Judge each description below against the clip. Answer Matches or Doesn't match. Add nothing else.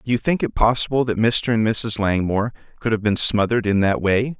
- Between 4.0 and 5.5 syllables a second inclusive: Doesn't match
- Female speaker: Doesn't match